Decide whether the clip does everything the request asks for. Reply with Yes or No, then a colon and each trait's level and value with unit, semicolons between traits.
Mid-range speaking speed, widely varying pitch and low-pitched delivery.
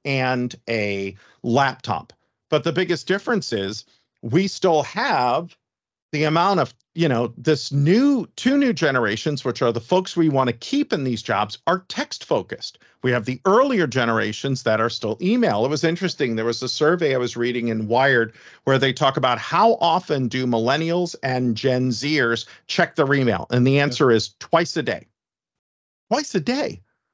Yes: average, 175 wpm; wide, 6.1 semitones; low, 130 Hz